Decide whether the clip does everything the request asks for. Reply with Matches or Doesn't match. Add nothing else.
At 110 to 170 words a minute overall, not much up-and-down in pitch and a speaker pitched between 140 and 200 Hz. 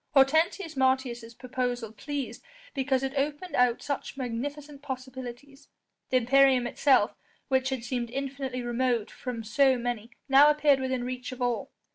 Doesn't match